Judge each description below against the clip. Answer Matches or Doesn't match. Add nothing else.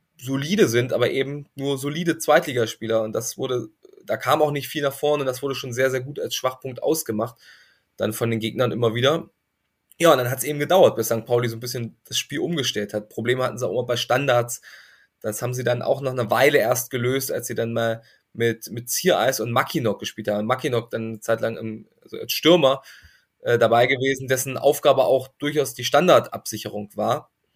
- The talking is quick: Matches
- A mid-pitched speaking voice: Doesn't match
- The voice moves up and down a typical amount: Matches